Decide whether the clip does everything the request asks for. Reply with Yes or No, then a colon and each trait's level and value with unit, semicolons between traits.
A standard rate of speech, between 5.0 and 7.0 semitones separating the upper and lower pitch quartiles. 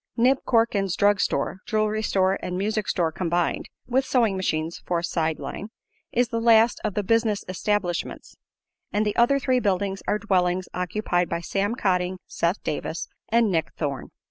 No: average, 170 wpm; average, 3.9 semitones